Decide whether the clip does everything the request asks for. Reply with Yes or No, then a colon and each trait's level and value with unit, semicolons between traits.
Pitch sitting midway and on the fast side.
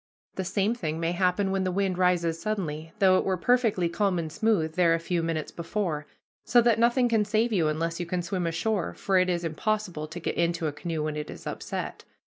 Yes: medium, 180 Hz; fast, 225 wpm